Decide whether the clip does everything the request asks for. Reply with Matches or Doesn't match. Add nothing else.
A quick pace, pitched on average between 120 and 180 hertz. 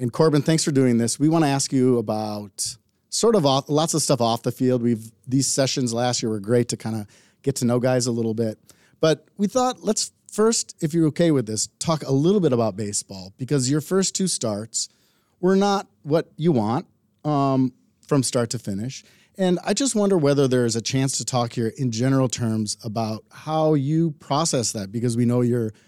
Matches